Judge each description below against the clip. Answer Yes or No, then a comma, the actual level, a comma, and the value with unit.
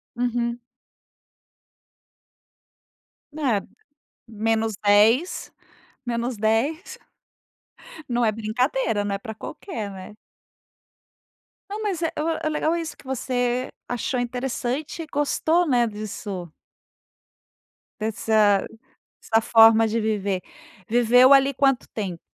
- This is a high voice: Yes, high, 235 Hz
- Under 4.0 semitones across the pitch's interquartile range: Yes, average, 3.6 semitones